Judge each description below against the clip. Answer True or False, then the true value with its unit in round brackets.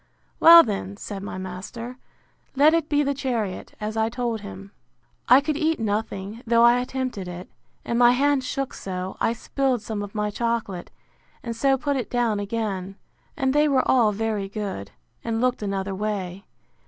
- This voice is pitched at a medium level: False (225 Hz)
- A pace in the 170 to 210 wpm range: True (175 wpm)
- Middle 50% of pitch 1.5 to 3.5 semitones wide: False (4.3 semitones)